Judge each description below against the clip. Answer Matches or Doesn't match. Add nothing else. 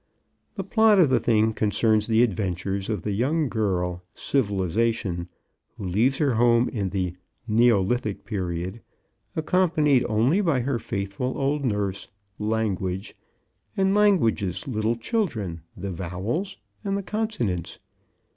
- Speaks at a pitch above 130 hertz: Doesn't match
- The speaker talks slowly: Matches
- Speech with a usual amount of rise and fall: Doesn't match